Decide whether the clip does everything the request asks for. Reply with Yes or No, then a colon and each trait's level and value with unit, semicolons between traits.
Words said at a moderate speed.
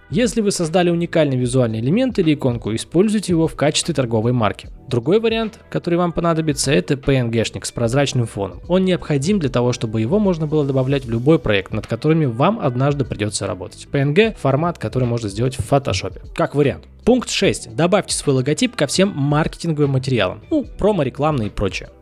No: fast, 175 wpm